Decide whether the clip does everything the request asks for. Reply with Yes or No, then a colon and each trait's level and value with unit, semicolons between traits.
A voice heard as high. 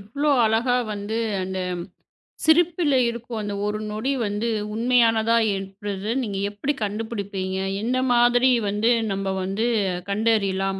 Yes: high, 215 Hz